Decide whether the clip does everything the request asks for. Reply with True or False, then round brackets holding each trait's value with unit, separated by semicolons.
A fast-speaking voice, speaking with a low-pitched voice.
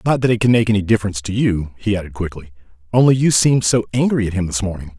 True (255 wpm; 105 Hz)